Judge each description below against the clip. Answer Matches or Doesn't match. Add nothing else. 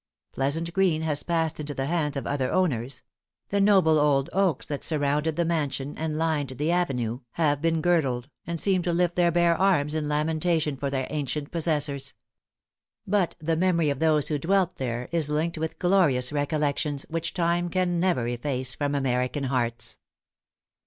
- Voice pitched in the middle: Matches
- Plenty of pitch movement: Doesn't match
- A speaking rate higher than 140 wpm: Matches